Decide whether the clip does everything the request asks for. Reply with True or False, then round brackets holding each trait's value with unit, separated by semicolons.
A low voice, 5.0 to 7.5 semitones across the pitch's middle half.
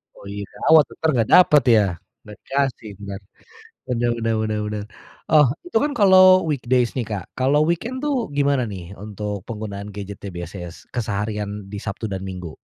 True (110 Hz; 5.4 semitones)